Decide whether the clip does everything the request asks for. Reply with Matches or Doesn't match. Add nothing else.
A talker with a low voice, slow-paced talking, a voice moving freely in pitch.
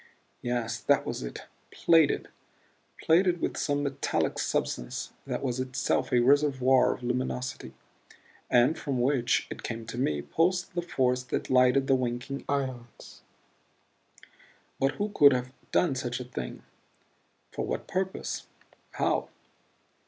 Doesn't match